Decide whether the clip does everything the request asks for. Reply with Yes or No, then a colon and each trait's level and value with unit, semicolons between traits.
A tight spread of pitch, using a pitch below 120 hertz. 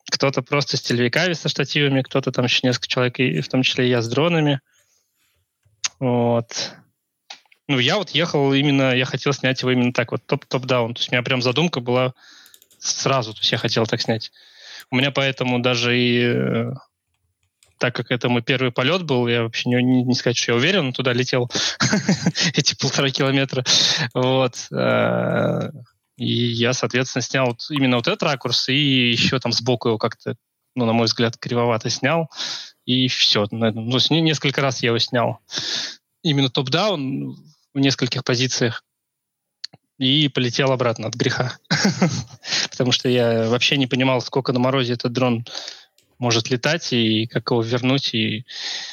No: narrow, 2.3 semitones; low, 130 Hz